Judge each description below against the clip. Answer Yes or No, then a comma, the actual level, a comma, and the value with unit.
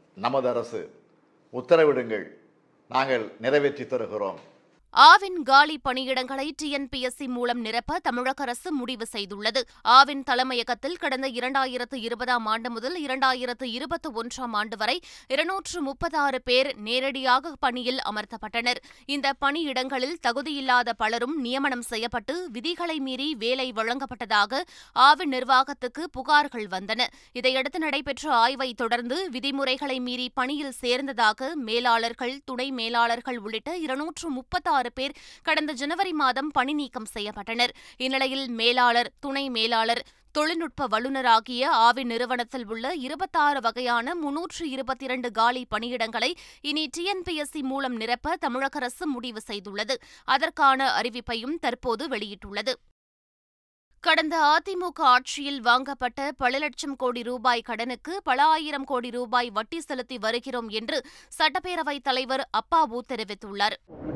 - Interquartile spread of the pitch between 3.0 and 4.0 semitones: Yes, average, 3.3 semitones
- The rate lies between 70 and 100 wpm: No, average, 110 wpm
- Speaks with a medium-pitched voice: No, very high, 260 Hz